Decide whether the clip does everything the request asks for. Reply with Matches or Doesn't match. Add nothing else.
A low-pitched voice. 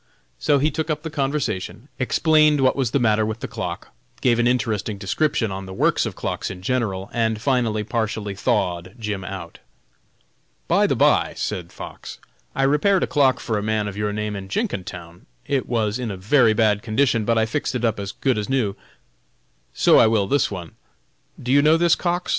Matches